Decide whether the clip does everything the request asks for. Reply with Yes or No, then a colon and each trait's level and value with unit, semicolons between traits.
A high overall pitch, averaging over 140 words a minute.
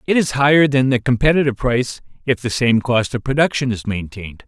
No: low, 125 Hz; average, 200 wpm